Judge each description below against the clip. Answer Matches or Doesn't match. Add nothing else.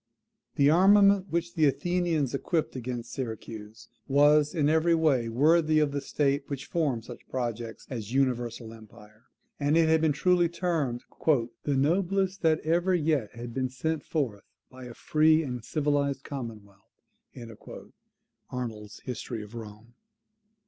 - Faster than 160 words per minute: Doesn't match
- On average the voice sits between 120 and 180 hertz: Matches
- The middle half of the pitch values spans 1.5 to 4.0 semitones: Doesn't match